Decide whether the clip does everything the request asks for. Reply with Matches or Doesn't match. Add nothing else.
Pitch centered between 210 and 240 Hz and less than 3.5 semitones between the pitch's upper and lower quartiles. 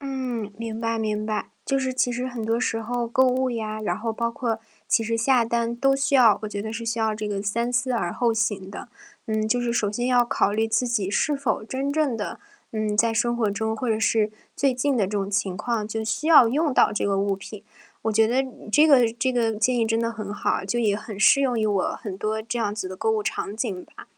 Matches